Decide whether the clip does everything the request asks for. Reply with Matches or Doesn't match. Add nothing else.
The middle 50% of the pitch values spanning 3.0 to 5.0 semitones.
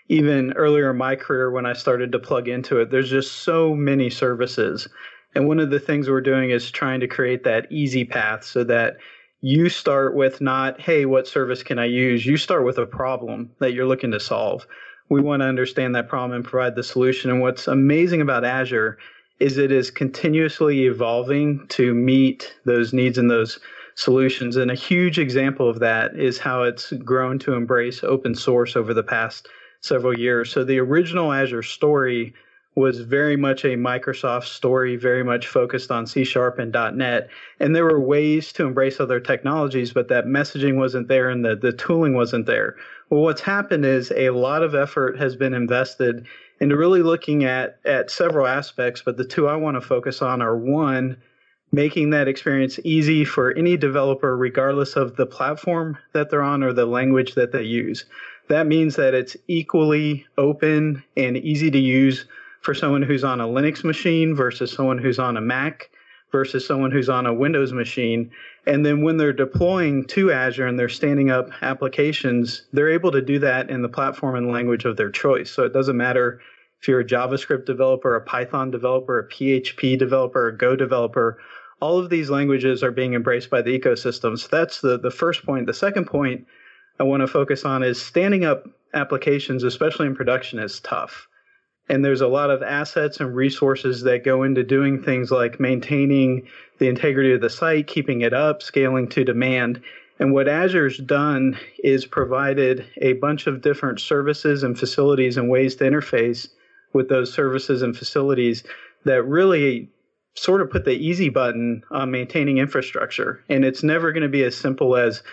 Doesn't match